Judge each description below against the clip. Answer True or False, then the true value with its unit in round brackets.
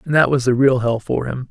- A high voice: False (125 Hz)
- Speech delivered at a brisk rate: True (320 wpm)